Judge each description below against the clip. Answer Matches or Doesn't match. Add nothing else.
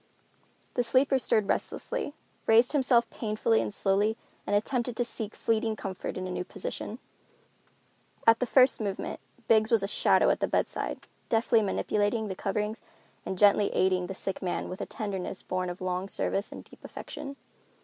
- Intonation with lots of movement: Doesn't match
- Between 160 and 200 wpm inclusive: Matches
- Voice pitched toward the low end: Doesn't match